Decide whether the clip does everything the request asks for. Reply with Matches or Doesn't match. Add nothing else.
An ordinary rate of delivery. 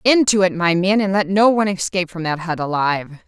Doesn't match